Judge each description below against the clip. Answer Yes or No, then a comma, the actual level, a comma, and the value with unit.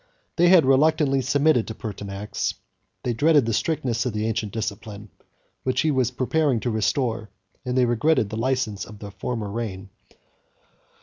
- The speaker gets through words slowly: No, average, 160 wpm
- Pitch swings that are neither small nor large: Yes, average, 3.9 semitones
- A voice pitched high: No, low, 120 Hz